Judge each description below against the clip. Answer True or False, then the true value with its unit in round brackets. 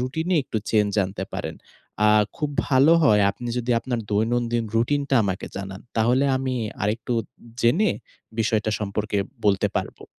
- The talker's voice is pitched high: False (115 Hz)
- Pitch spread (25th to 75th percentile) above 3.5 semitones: True (3.9 semitones)